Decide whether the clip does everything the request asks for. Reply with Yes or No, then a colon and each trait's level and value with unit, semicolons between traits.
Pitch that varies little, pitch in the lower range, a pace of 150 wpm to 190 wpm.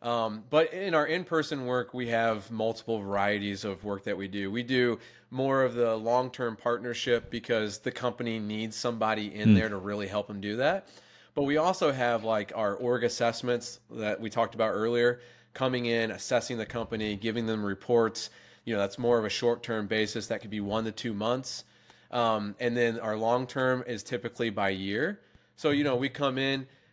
No: narrow, 2.3 semitones; low, 115 Hz; average, 200 wpm